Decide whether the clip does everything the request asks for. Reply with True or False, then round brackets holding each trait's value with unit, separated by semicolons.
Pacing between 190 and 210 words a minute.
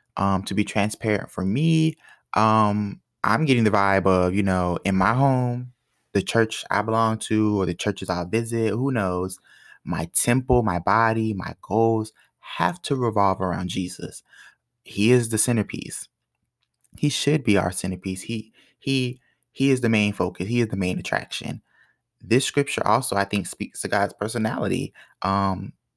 False (165 wpm)